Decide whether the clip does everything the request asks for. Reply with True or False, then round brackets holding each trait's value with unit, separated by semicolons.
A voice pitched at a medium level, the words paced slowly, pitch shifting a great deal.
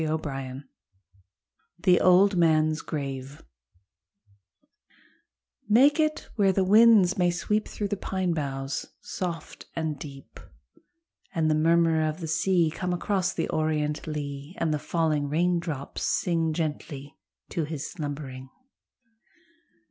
False (160 Hz; 120 wpm; 3.3 semitones)